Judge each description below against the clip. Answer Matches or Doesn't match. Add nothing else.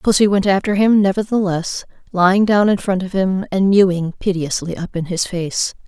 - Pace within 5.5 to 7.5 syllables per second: Doesn't match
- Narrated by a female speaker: Matches